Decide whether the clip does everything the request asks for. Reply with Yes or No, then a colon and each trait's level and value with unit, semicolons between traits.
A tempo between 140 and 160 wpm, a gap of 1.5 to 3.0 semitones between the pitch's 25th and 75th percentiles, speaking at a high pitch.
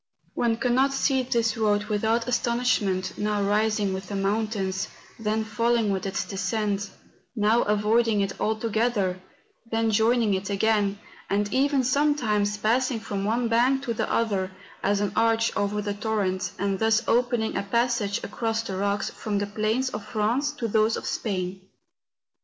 Yes: average, 155 wpm; narrow, 2.4 semitones; high, 215 Hz